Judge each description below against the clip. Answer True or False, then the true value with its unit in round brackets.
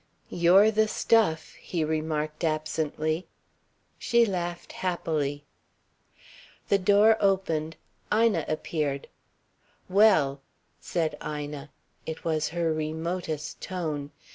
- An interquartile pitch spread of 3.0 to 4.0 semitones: True (3.3 semitones)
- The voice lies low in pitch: False (160 Hz)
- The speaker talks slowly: True (90 wpm)